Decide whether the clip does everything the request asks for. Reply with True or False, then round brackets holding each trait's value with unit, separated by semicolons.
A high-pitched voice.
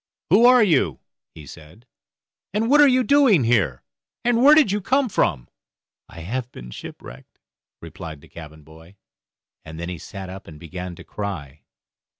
False (95 Hz)